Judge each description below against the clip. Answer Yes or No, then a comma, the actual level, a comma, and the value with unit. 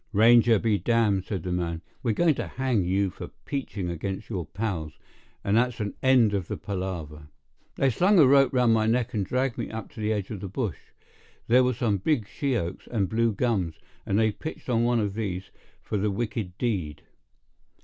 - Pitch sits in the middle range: No, low, 110 Hz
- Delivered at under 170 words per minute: No, average, 200 wpm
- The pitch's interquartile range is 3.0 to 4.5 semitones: Yes, average, 4.0 semitones